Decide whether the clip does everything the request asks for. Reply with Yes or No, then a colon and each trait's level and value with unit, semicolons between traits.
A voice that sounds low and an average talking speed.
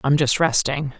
No: medium, 145 Hz; average, 180 wpm